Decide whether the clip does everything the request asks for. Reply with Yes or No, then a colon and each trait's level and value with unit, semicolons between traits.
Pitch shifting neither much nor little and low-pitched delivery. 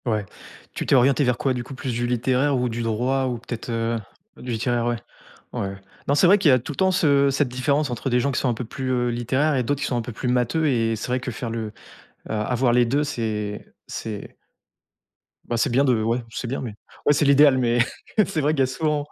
Yes: average, 3.0 semitones; low, 125 Hz